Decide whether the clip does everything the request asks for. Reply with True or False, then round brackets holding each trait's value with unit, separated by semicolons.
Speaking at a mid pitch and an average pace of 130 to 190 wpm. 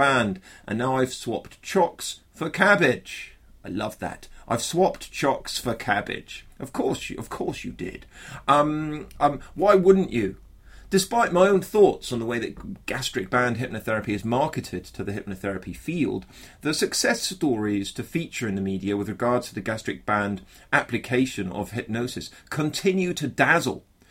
False (120 Hz; 160 wpm)